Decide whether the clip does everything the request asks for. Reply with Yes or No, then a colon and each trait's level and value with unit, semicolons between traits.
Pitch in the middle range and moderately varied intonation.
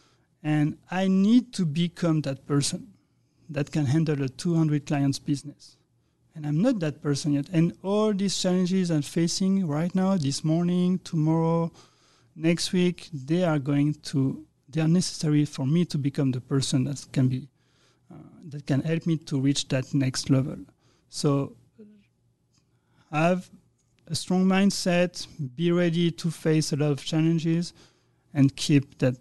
Yes: medium, 155 Hz; average, 3.6 semitones